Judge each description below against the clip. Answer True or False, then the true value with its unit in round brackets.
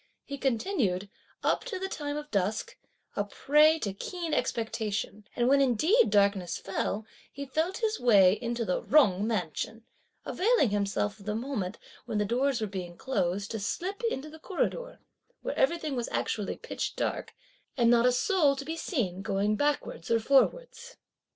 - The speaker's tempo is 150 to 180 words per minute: True (165 wpm)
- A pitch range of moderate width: False (7.0 semitones)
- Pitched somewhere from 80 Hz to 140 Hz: False (240 Hz)